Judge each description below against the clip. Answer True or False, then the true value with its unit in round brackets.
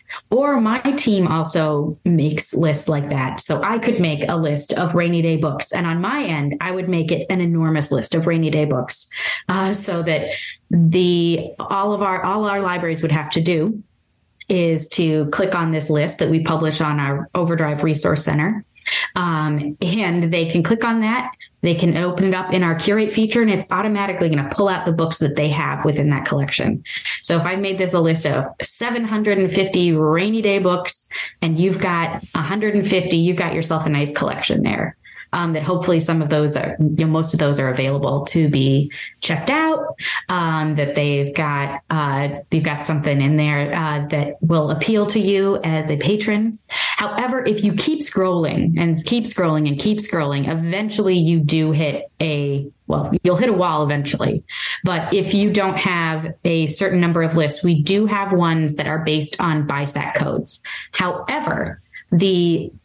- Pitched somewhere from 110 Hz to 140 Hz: False (165 Hz)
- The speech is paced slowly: False (185 wpm)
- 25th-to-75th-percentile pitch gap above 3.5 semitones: True (3.9 semitones)